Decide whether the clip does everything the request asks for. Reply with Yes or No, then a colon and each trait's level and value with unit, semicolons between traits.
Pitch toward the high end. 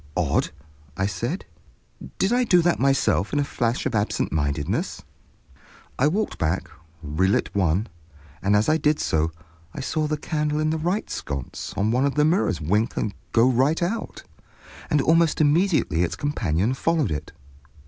No: low, 135 Hz